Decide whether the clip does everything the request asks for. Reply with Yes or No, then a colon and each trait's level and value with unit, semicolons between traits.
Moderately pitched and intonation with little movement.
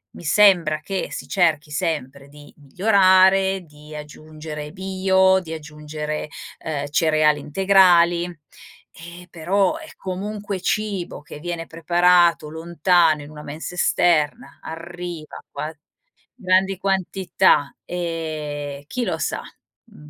No: medium, 170 Hz; average, 3.8 semitones